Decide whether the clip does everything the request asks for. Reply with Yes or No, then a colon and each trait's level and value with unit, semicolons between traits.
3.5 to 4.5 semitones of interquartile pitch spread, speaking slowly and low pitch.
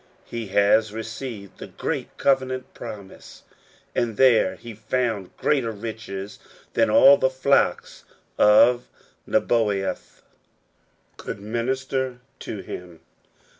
Yes: average, 4.0 semitones; slow, 100 wpm; low, 115 Hz